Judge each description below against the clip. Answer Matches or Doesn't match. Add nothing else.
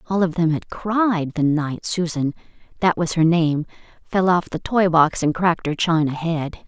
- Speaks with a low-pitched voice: Doesn't match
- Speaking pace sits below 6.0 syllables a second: Matches